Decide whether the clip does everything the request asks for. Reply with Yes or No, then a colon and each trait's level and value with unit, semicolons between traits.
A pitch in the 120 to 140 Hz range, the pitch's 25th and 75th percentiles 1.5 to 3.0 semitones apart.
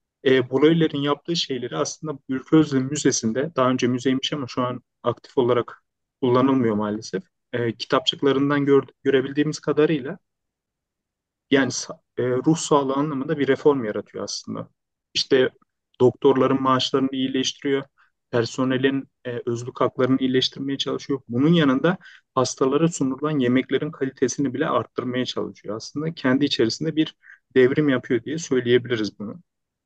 Yes: low, 135 Hz; narrow, 2.4 semitones